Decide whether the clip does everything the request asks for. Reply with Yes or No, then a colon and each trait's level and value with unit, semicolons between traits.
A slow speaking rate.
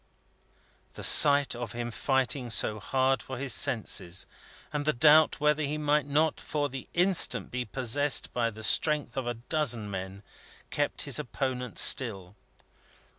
No: average, 150 wpm